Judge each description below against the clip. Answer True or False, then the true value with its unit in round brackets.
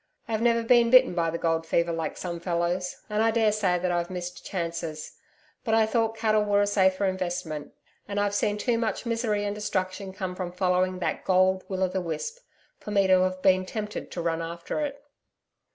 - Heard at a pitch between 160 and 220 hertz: True (190 Hz)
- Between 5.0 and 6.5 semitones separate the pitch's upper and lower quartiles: False (3.3 semitones)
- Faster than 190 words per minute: True (200 wpm)